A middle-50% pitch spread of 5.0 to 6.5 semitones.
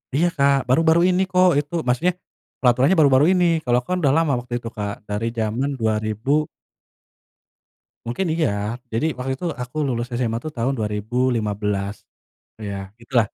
Yes: wide, 5.5 semitones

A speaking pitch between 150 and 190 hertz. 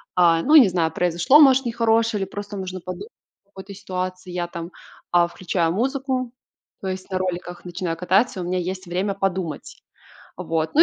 Yes: medium, 185 Hz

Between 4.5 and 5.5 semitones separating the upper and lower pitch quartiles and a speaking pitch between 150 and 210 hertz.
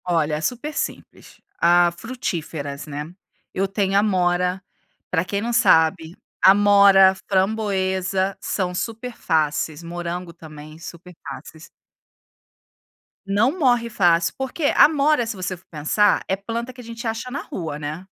Yes: average, 4.8 semitones; high, 190 Hz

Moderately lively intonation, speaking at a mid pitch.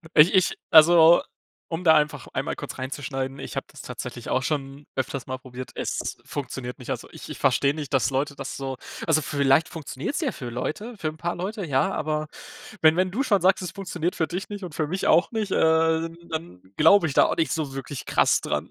Yes: average, 4.4 semitones; medium, 155 Hz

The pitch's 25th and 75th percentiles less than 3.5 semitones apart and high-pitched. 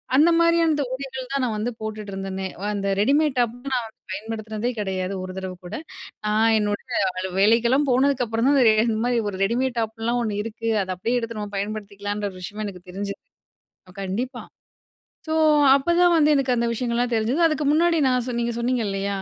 No: average, 4.0 semitones; high, 225 Hz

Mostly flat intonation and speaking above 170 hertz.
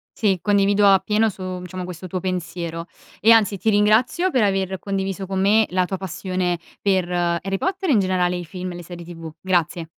Yes: narrow, 2.3 semitones; high, 190 Hz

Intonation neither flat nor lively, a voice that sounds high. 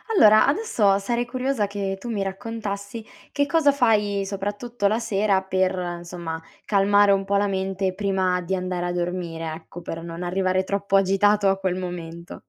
No: narrow, 2.2 semitones; high, 195 Hz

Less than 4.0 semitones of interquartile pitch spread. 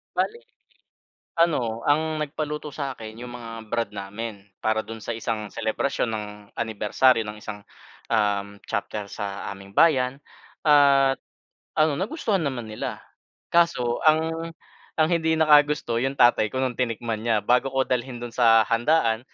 No: average, 5.1 semitones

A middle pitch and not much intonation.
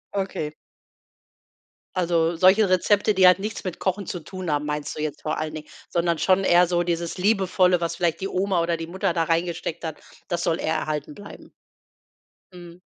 Yes: medium, 175 Hz; narrow, 2.2 semitones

